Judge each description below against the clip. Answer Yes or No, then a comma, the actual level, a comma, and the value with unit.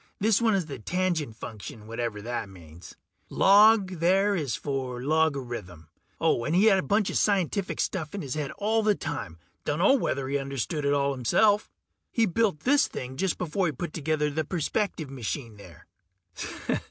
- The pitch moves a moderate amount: No, wide, 7.5 semitones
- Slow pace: No, average, 175 wpm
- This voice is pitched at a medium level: Yes, medium, 150 Hz